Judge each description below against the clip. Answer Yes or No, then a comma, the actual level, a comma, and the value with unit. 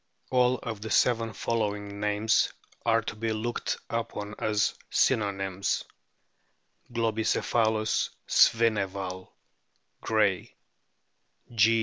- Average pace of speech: No, slow, 85 wpm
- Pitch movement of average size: No, narrow, 1.9 semitones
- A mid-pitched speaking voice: No, low, 110 Hz